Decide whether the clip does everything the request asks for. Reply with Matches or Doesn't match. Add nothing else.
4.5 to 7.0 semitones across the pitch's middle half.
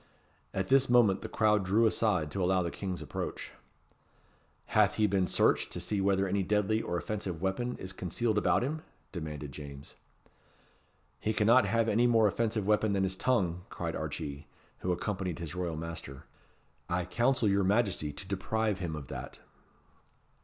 Doesn't match